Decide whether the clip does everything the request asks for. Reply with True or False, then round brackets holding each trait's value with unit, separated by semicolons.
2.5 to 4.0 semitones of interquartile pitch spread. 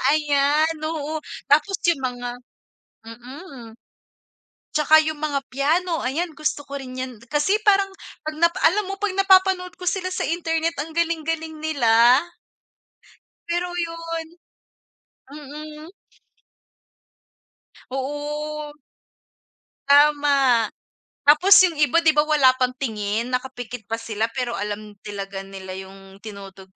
False (4.9 semitones)